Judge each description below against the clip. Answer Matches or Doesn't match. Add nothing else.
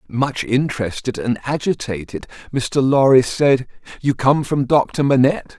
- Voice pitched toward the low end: Matches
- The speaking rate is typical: Doesn't match